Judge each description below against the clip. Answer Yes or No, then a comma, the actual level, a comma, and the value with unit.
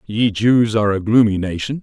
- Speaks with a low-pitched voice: Yes, low, 110 Hz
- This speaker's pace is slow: No, average, 200 wpm